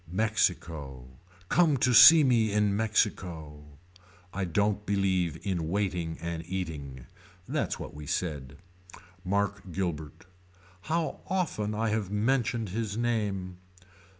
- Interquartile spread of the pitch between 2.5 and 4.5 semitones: No, average, 5.0 semitones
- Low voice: Yes, low, 100 Hz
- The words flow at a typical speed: No, slow, 115 wpm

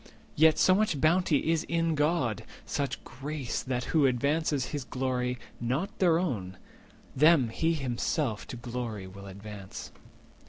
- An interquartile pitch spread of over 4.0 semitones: Yes, average, 5.1 semitones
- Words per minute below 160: Yes, slow, 135 wpm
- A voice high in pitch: No, low, 135 Hz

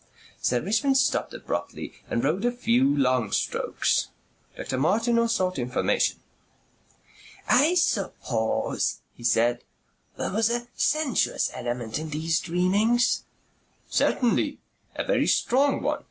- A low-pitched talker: No, medium, 185 Hz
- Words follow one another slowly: Yes, slow, 115 wpm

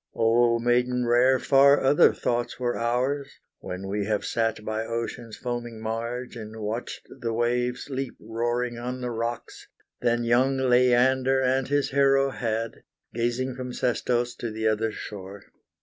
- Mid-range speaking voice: No, low, 120 Hz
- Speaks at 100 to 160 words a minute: Yes, average, 150 wpm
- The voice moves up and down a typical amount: No, narrow, 1.9 semitones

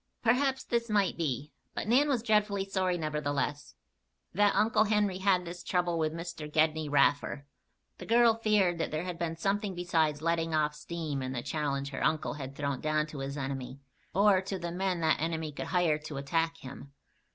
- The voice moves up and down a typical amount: Yes, average, 4.5 semitones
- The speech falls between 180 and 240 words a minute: Yes, average, 185 wpm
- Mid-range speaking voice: Yes, medium, 165 Hz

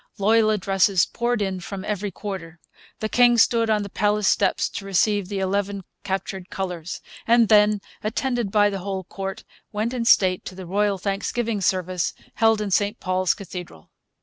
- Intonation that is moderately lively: No, narrow, 2.2 semitones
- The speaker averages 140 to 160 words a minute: No, average, 170 wpm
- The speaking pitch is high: Yes, high, 200 Hz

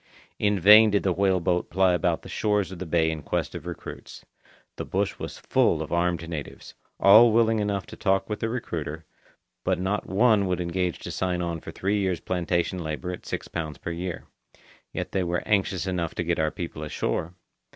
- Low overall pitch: Yes, very low, 90 Hz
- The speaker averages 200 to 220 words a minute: Yes, fast, 205 wpm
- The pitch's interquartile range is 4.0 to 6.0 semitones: No, average, 2.7 semitones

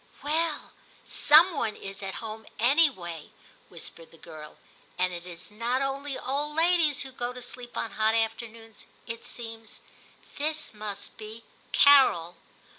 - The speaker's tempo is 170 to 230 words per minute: No, average, 145 wpm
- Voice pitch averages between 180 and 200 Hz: No, high, 230 Hz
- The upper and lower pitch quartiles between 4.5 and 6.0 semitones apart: Yes, average, 5.2 semitones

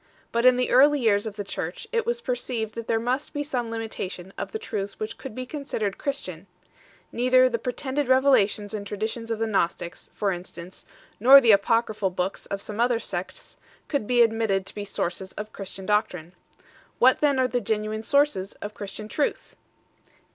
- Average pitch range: Yes, average, 4.1 semitones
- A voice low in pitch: No, high, 225 Hz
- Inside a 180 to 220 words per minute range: Yes, average, 185 wpm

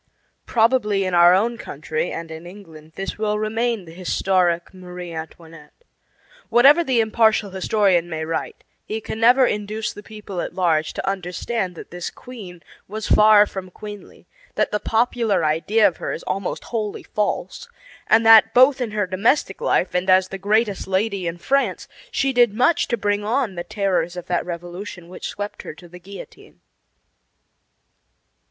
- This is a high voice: Yes, high, 200 Hz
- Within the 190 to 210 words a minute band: No, average, 165 wpm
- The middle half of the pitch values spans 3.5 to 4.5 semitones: Yes, average, 3.9 semitones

